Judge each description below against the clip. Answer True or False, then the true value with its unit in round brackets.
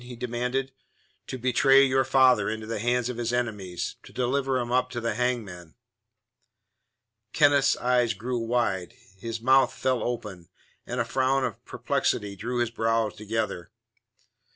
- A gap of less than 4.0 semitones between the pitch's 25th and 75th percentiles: True (2.4 semitones)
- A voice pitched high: False (120 Hz)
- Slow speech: False (150 wpm)